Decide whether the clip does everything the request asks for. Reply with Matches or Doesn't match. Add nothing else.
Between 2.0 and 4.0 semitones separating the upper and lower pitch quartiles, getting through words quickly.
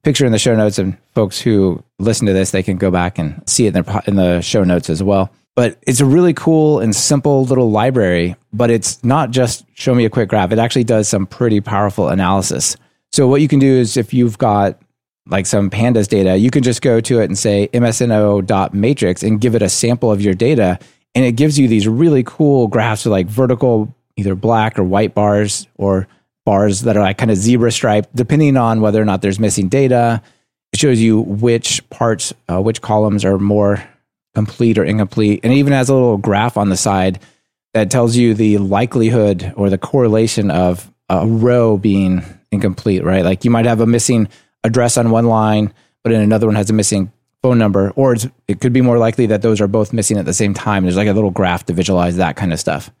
Matches